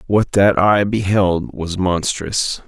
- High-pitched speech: No, very low, 95 Hz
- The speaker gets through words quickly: No, slow, 135 wpm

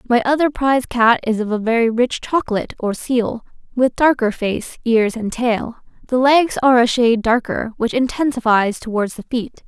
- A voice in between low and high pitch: No, high, 240 Hz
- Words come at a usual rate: Yes, average, 180 wpm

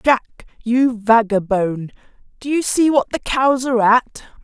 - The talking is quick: No, average, 150 wpm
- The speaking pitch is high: Yes, high, 240 Hz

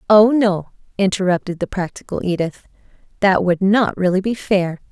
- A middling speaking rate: Yes, average, 145 wpm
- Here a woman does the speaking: Yes, female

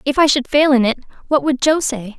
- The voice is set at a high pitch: Yes, very high, 270 Hz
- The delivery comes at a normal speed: No, fast, 275 wpm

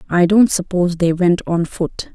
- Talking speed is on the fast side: No, average, 195 wpm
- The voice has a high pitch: No, medium, 180 Hz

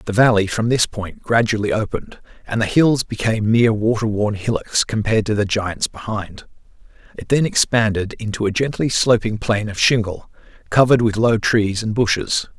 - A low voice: Yes, low, 110 Hz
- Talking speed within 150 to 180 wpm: Yes, average, 170 wpm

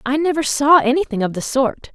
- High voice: Yes, very high, 275 Hz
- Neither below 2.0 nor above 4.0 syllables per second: No, 5.4 syllables/s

